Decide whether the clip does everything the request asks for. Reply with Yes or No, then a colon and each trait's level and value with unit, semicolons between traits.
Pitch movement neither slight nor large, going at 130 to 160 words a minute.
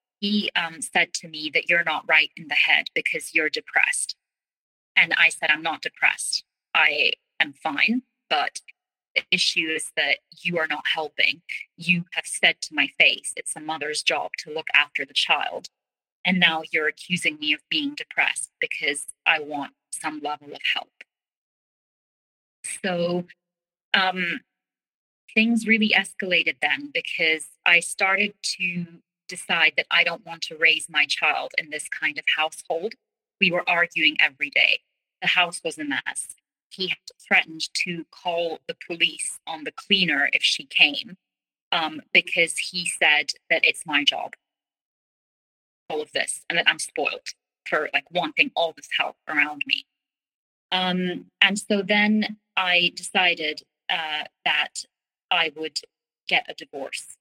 Yes: average, 4.6 semitones; average, 155 wpm